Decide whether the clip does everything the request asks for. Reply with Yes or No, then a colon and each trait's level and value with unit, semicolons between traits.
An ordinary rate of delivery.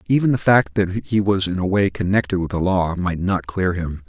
No: fast, 250 wpm